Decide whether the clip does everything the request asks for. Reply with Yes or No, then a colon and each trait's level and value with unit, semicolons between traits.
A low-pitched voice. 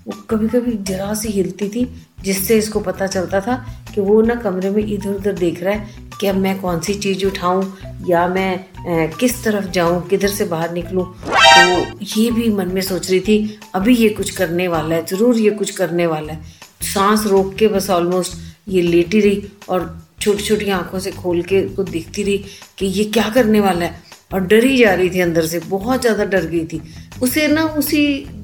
No: high, 195 Hz